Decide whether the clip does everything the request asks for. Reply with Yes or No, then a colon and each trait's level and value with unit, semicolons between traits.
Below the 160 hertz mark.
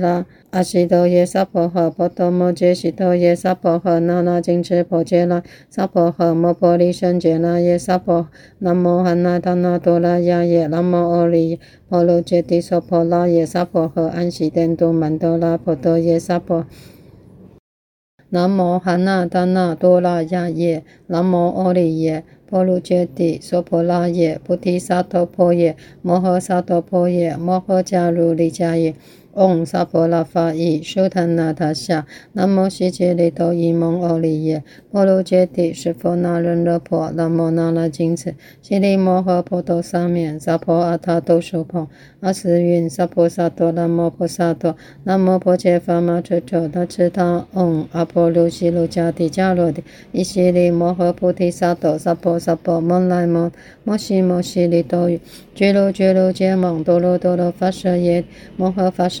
No: medium, 175 Hz